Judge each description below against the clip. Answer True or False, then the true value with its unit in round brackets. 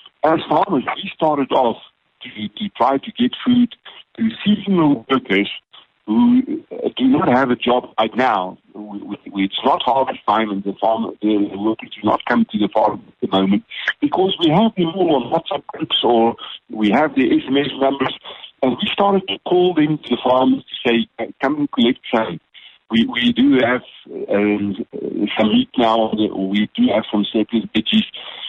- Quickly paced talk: False (180 wpm)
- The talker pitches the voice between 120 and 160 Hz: True (135 Hz)